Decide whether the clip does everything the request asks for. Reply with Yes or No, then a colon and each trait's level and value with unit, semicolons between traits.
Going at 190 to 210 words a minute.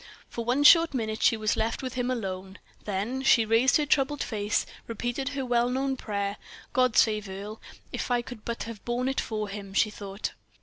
Yes: average, 200 wpm